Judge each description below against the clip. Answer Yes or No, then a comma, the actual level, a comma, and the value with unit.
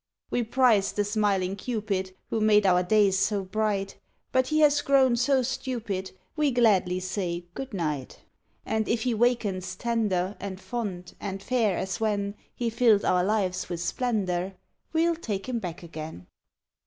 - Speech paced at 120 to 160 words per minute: Yes, average, 155 wpm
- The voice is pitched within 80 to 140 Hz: No, high, 205 Hz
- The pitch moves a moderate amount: Yes, average, 4.2 semitones